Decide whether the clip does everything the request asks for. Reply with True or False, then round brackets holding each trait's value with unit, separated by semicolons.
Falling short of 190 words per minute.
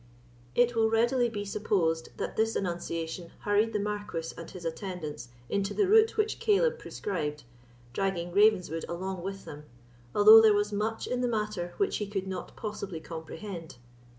True (160 wpm)